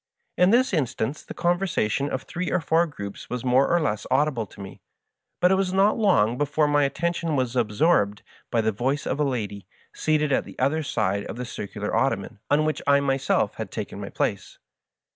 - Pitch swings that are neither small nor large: No, wide, 5.8 semitones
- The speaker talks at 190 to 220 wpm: Yes, average, 200 wpm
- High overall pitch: No, medium, 140 Hz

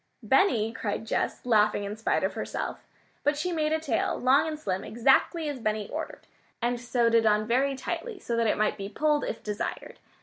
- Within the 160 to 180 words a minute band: No, average, 200 wpm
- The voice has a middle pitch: No, high, 235 Hz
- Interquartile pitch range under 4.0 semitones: No, wide, 5.4 semitones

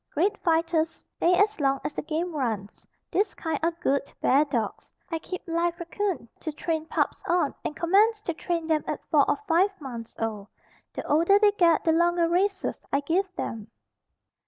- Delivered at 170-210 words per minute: Yes, average, 180 wpm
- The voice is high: Yes, very high, 330 Hz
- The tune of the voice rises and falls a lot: No, average, 3.5 semitones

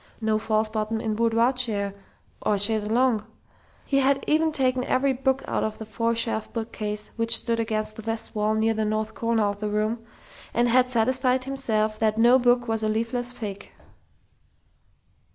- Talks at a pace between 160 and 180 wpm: Yes, average, 175 wpm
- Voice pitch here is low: No, high, 225 Hz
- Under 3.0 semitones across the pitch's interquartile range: Yes, narrow, 2.5 semitones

